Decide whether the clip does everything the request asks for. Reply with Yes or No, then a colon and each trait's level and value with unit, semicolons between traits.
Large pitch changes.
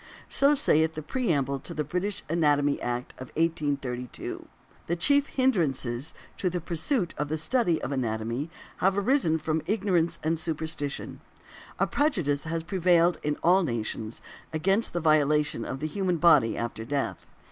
No: average, 4.1 semitones